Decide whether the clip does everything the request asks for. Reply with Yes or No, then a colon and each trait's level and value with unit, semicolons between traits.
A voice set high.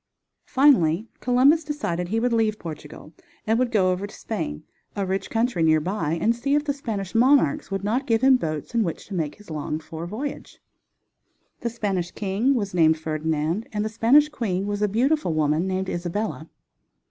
Yes: high, 205 Hz